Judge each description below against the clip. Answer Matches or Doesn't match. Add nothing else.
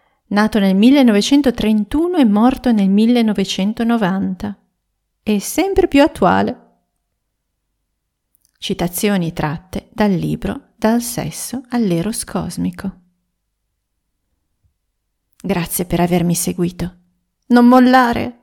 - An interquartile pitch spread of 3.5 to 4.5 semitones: Doesn't match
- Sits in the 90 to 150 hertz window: Doesn't match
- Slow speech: Matches